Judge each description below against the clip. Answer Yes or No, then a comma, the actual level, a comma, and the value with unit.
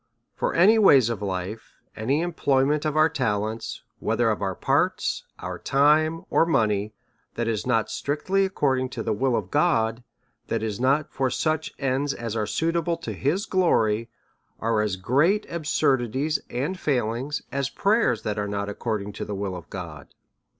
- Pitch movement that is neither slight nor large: No, wide, 6.1 semitones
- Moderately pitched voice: No, low, 130 Hz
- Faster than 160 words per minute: Yes, average, 170 wpm